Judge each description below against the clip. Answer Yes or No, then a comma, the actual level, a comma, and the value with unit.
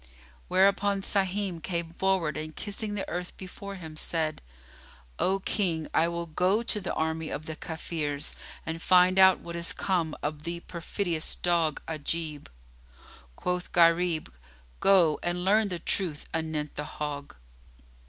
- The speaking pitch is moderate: Yes, medium, 170 Hz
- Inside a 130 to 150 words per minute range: Yes, average, 145 wpm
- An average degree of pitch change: Yes, average, 3.0 semitones